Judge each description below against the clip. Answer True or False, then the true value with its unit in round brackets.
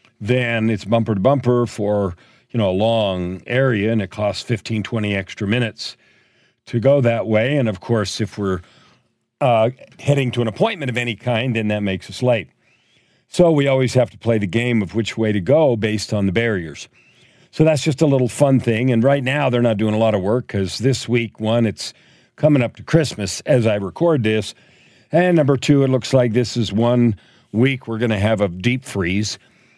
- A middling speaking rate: False (210 wpm)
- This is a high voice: False (115 Hz)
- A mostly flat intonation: False (3.4 semitones)